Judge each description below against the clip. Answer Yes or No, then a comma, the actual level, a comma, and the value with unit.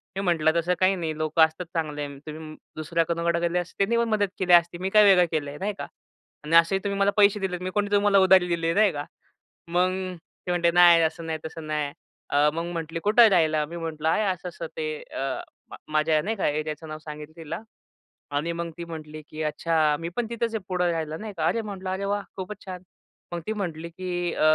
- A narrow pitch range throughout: No, average, 3.2 semitones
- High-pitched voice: No, medium, 170 Hz